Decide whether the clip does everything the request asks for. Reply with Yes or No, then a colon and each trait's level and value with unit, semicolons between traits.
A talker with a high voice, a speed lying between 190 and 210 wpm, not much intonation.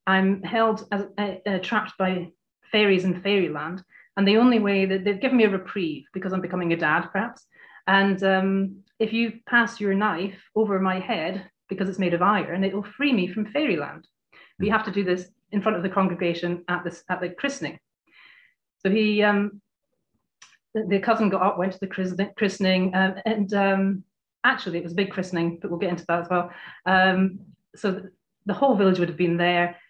Yes: high, 195 Hz; average, 200 wpm; narrow, 2.3 semitones